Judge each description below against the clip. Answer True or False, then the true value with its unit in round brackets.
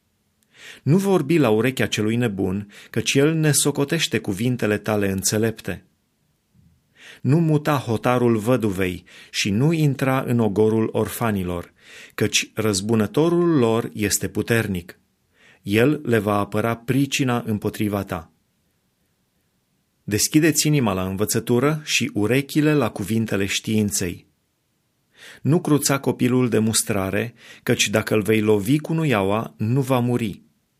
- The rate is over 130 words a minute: False (115 wpm)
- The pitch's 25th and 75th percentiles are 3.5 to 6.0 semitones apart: True (4.6 semitones)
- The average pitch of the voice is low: True (115 Hz)